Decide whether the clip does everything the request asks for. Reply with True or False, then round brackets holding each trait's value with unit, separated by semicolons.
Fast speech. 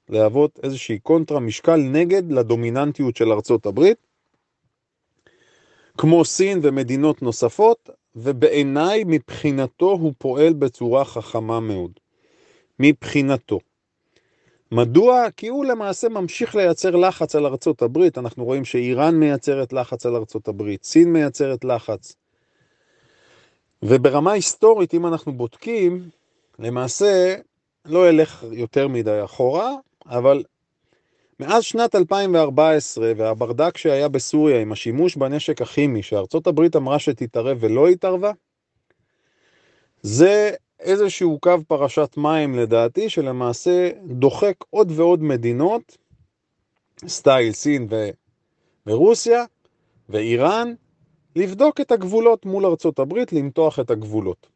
False (105 wpm)